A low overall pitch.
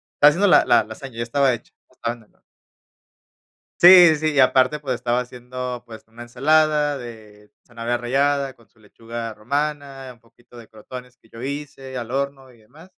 Yes: low, 125 Hz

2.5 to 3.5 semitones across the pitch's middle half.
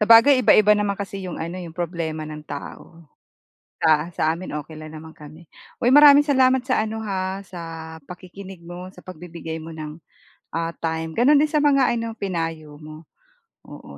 No: average, 5.2 semitones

